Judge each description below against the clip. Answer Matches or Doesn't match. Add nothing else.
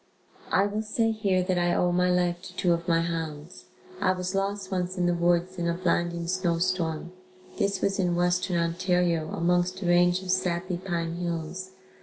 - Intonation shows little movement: Matches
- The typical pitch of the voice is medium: Matches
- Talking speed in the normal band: Matches